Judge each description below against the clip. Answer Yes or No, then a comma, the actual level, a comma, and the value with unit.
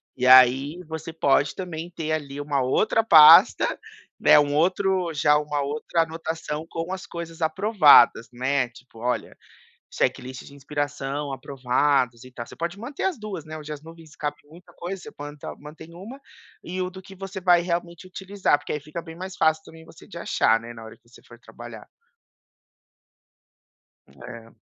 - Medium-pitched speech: Yes, medium, 155 Hz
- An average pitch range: Yes, average, 4.0 semitones